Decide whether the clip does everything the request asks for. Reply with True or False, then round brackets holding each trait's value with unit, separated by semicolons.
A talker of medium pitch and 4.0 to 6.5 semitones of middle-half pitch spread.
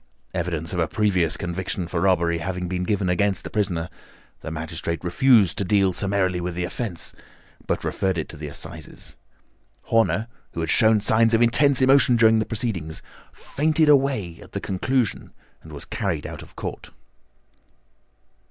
False (95 Hz; 4.5 semitones)